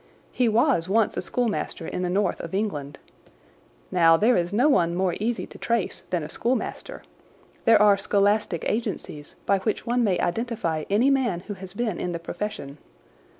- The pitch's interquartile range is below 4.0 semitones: No, average, 4.8 semitones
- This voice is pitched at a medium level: No, high, 200 Hz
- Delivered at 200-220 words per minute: No, average, 175 wpm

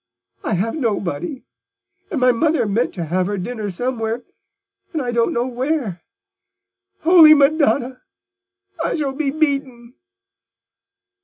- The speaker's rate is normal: No, slow, 125 wpm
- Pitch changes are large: No, average, 4.6 semitones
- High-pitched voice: Yes, very high, 250 Hz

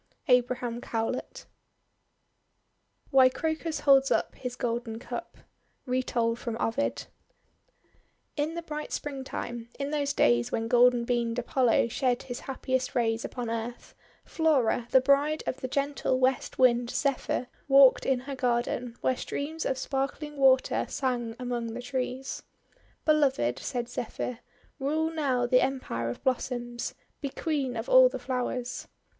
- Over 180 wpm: No, average, 140 wpm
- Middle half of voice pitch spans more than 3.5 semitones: No, narrow, 2.5 semitones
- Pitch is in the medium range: No, very high, 255 Hz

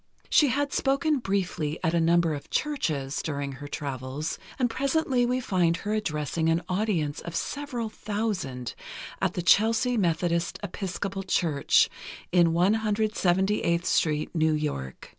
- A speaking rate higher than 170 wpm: No, slow, 135 wpm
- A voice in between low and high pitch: Yes, medium, 180 Hz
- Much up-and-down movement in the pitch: Yes, wide, 5.9 semitones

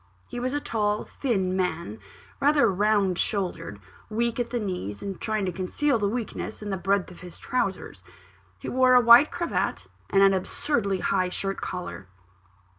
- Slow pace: No, average, 170 wpm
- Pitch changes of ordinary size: Yes, average, 4.3 semitones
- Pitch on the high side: Yes, high, 200 Hz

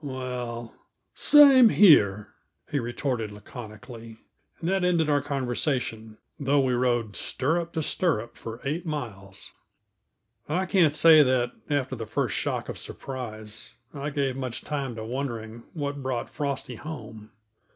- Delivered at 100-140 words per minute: Yes, slow, 135 wpm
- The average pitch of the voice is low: Yes, low, 130 Hz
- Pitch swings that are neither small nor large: Yes, average, 4.3 semitones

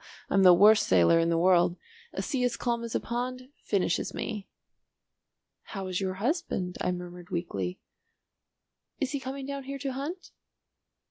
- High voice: Yes, high, 205 Hz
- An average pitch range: No, wide, 6.6 semitones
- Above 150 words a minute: Yes, average, 160 wpm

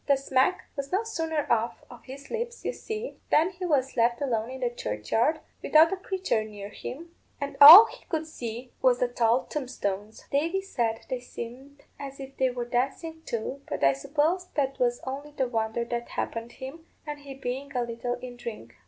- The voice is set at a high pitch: Yes, very high, 265 Hz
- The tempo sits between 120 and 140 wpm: No, average, 195 wpm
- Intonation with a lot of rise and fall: No, average, 4.5 semitones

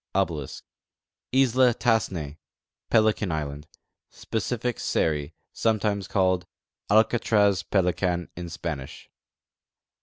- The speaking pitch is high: No, very low, 95 Hz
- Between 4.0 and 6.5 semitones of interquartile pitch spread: Yes, average, 5.0 semitones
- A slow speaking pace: Yes, slow, 85 wpm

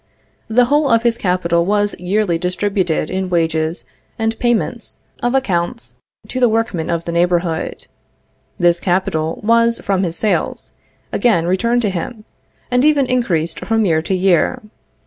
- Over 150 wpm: No, average, 145 wpm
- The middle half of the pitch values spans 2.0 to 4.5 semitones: No, average, 5.3 semitones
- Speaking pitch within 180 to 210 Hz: Yes, high, 190 Hz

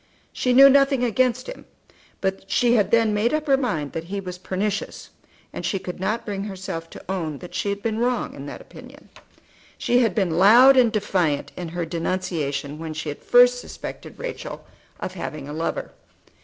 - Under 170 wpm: No, average, 190 wpm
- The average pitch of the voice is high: Yes, high, 200 Hz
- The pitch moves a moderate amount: No, wide, 6.1 semitones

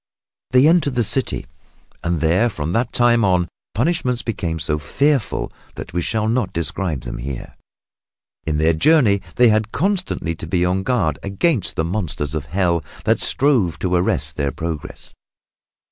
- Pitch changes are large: Yes, wide, 6.9 semitones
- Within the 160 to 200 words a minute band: Yes, average, 170 wpm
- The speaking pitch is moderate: No, very low, 95 Hz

